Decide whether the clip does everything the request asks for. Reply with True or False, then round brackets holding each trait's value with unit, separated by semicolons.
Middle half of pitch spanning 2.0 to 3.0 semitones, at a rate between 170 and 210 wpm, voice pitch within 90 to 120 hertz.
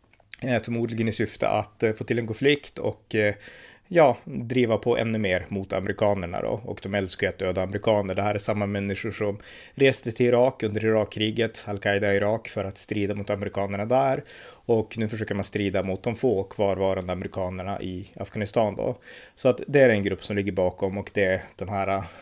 True (2.4 semitones; 190 wpm; 105 Hz)